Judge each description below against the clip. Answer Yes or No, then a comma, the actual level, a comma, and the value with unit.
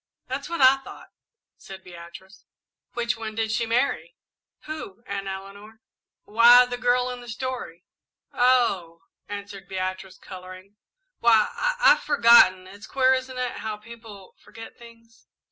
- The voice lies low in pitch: No, high, 225 Hz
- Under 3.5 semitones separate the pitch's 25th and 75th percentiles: No, average, 4.3 semitones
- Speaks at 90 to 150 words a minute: Yes, average, 140 wpm